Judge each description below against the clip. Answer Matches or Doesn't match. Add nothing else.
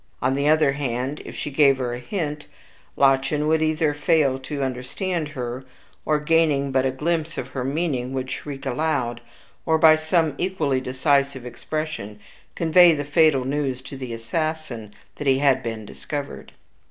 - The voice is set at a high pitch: Doesn't match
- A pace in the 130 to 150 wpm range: Doesn't match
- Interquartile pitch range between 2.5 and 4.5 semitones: Matches